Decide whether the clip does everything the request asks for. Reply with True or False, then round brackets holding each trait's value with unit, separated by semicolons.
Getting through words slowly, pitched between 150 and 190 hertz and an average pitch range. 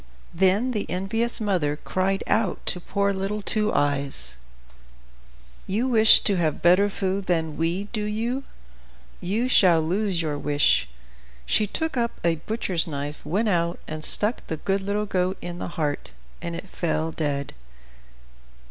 False (150 wpm; 185 Hz; 4.6 semitones)